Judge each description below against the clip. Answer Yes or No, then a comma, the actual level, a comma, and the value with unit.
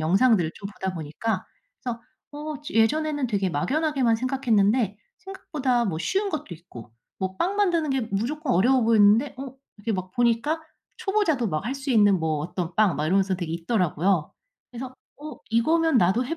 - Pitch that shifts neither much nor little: No, wide, 7.1 semitones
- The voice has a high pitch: Yes, high, 230 Hz